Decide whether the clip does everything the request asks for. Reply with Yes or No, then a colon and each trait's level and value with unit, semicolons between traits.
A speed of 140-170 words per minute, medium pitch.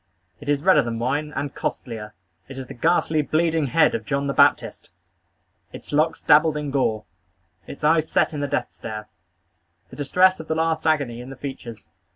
No: average, 190 wpm; medium, 145 Hz